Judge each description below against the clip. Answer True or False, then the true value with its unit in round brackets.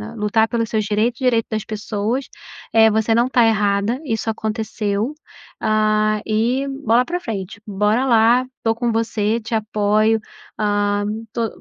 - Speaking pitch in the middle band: False (220 Hz)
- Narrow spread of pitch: True (1.6 semitones)